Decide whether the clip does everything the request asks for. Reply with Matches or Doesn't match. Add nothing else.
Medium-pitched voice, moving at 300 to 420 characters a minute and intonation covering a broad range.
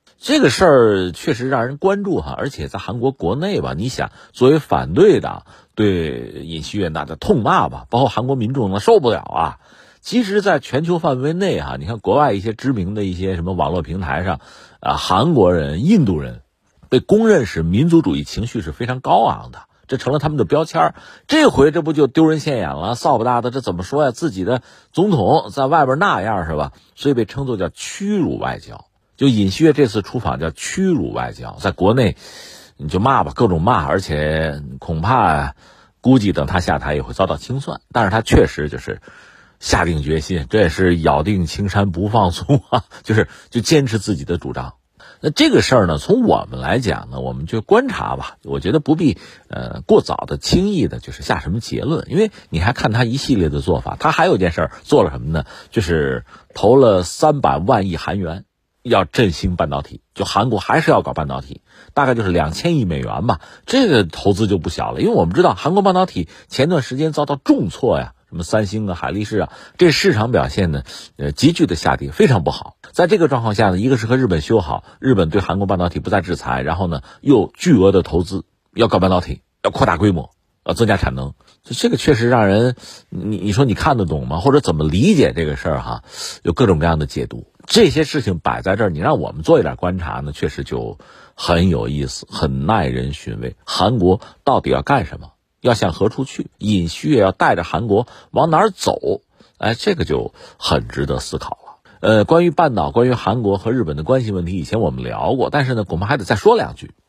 Doesn't match